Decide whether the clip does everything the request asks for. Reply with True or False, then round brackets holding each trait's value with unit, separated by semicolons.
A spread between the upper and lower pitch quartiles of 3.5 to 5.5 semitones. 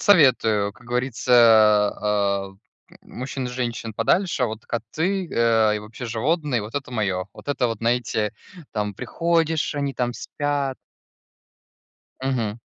True (4.2 semitones)